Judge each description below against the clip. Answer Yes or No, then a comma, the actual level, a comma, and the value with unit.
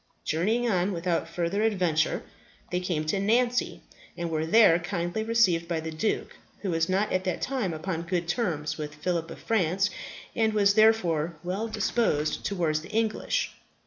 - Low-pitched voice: No, medium, 180 Hz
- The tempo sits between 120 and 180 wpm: Yes, average, 165 wpm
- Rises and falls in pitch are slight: No, average, 4.6 semitones